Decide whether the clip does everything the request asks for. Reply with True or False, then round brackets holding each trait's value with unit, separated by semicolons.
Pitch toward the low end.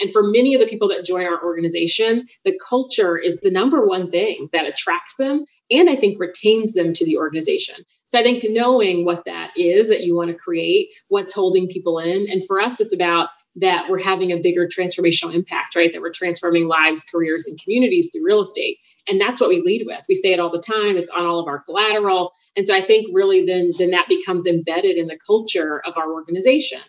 False (185 Hz)